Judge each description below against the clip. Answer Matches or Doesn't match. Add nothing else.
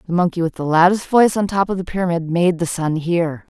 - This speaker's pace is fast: Matches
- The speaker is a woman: Matches